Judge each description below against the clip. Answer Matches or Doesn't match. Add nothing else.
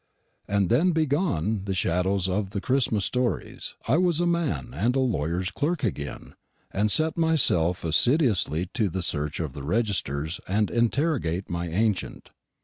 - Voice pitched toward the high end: Doesn't match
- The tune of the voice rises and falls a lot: Matches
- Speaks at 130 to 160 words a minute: Matches